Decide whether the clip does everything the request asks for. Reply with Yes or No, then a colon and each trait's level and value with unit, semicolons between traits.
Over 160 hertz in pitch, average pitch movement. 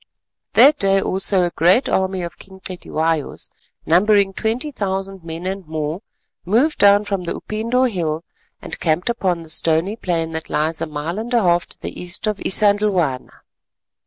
Yes: medium, 185 Hz; average, 3.8 semitones